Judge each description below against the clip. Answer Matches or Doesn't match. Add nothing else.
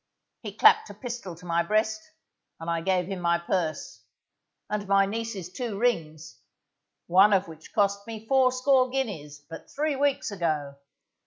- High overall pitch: Matches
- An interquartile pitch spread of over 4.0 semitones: Matches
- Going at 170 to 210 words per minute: Doesn't match